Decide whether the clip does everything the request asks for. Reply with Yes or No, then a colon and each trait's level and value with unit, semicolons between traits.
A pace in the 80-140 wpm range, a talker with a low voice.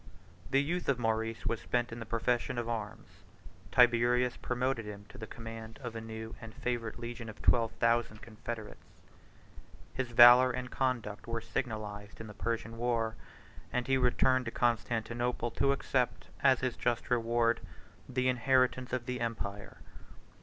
No: average, 155 wpm; low, 120 Hz